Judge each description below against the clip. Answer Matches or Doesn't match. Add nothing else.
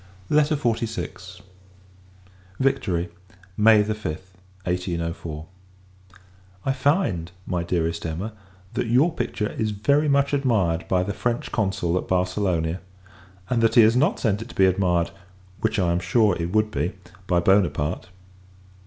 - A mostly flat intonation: Doesn't match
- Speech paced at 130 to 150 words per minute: Matches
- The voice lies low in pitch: Matches